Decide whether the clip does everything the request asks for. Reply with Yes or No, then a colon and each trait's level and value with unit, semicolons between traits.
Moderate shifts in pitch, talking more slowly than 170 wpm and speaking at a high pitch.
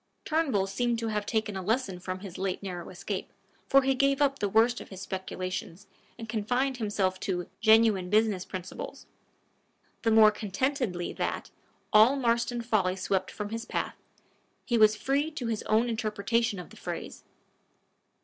Yes: average, 3.8 semitones; average, 160 wpm; high, 215 Hz